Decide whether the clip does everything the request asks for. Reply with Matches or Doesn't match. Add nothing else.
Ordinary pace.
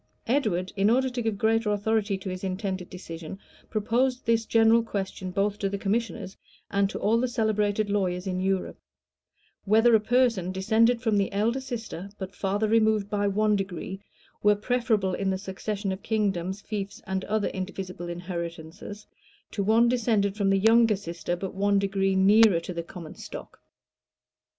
Matches